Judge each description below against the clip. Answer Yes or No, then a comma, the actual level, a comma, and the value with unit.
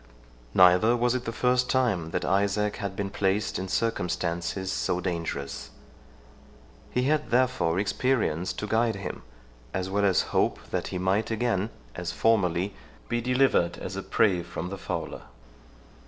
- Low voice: Yes, low, 100 Hz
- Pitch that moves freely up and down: No, average, 4.4 semitones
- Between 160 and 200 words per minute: No, average, 150 wpm